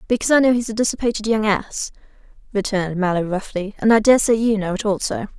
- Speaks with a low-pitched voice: No, high, 210 Hz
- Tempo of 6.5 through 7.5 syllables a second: Yes, 6.7 syllables/s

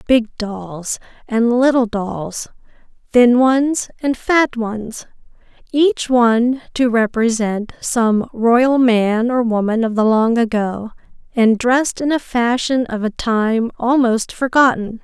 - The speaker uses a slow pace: Yes, slow, 130 wpm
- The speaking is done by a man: No, female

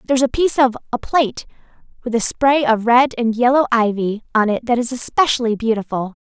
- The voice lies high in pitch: Yes, high, 240 Hz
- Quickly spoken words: No, average, 195 wpm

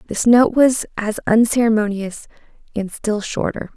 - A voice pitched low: No, high, 220 Hz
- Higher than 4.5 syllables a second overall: No, 4.4 syllables/s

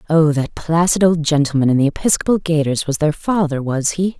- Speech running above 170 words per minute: Yes, average, 200 wpm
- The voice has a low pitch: No, medium, 160 Hz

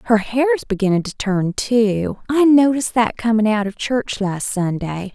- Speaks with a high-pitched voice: Yes, high, 220 Hz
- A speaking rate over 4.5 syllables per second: No, 4.3 syllables/s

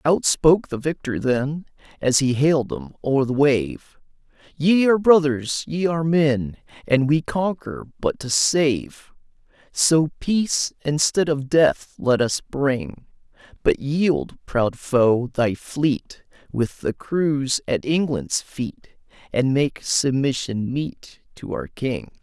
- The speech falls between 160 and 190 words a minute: No, average, 140 wpm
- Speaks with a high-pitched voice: No, medium, 145 Hz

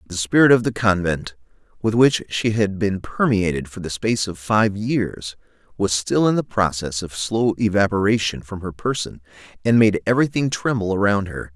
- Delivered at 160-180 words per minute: Yes, average, 175 wpm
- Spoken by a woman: No, male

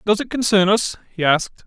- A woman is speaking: No, male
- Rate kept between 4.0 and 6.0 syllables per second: Yes, 5.6 syllables/s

